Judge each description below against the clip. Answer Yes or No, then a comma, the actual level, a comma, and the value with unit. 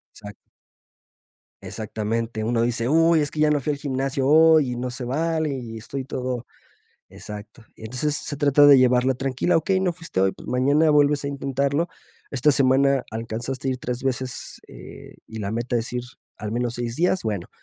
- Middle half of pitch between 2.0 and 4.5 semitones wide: Yes, average, 3.6 semitones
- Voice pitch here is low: Yes, low, 130 Hz